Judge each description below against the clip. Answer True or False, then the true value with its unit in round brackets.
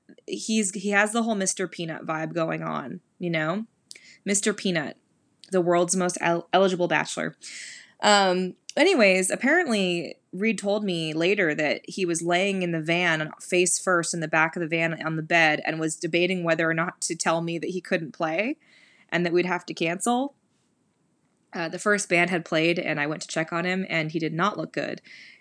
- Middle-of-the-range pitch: True (175 Hz)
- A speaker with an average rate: True (195 wpm)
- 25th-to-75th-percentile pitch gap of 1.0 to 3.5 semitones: True (2.9 semitones)